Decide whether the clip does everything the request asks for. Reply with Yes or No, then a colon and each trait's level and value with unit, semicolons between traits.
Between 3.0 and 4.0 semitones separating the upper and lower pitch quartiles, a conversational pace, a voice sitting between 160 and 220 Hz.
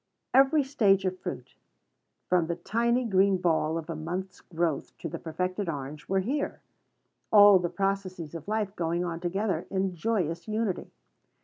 Yes: average, 3.4 semitones; average, 155 wpm; medium, 185 Hz